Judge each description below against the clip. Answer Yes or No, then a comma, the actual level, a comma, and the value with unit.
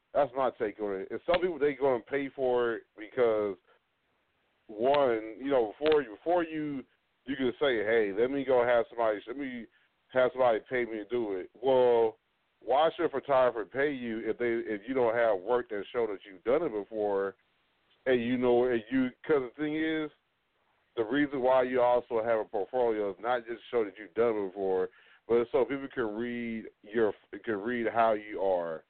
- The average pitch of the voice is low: Yes, low, 125 Hz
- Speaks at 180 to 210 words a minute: Yes, average, 200 wpm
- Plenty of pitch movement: No, average, 3.7 semitones